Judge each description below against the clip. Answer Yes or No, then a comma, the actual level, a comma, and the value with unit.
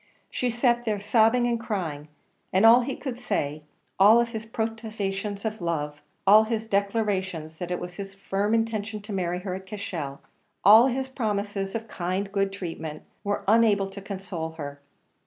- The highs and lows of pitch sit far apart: No, average, 3.4 semitones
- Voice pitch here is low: No, high, 200 Hz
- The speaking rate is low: No, average, 170 wpm